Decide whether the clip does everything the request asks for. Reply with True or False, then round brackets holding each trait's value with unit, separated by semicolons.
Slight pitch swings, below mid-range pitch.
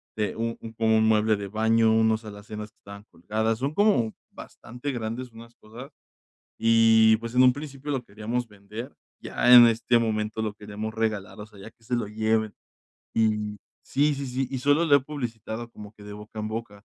True (2.3 semitones; 110 Hz)